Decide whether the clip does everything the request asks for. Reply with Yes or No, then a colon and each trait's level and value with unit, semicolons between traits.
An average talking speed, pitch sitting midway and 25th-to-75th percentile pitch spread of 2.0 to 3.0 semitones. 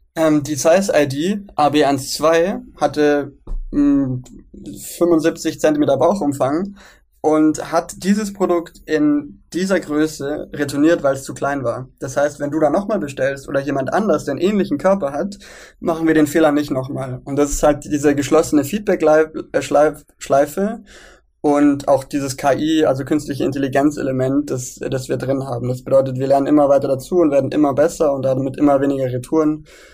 Yes: average, 160 wpm; medium, 145 Hz; narrow, 2.5 semitones